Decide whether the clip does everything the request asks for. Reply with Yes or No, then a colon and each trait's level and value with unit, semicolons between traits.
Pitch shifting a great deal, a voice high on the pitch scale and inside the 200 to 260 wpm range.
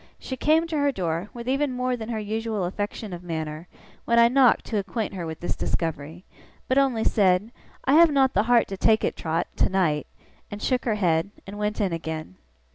Yes: wide, 5.9 semitones; high, 210 Hz; fast, 205 wpm